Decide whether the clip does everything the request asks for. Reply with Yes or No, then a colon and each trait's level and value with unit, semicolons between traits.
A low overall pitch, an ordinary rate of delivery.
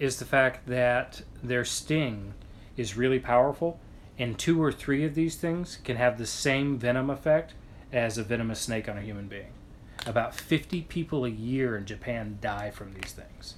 Yes: low, 125 Hz; average, 180 wpm